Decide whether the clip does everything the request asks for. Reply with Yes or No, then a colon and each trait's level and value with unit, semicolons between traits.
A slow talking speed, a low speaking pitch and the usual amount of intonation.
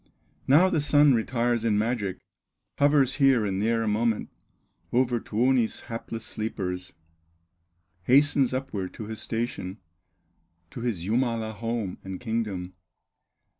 Yes: slow, 120 wpm; low, 115 Hz; average, 3.5 semitones